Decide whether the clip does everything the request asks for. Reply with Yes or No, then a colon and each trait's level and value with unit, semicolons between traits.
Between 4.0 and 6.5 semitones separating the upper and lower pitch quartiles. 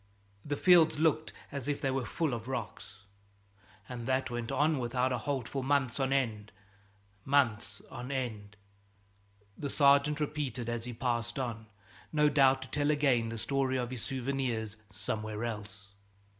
No: average, 3.4 semitones